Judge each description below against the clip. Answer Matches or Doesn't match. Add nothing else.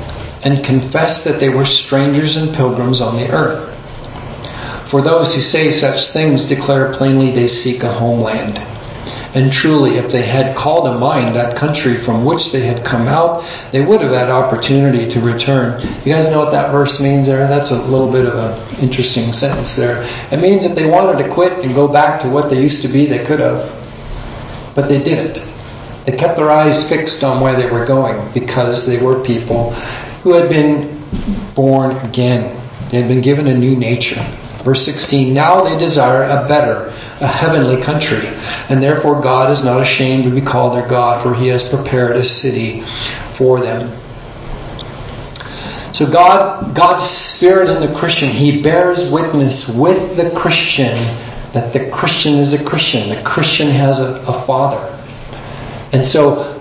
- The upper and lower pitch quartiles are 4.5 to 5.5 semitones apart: Doesn't match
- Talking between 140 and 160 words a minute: Doesn't match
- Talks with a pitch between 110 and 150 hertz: Matches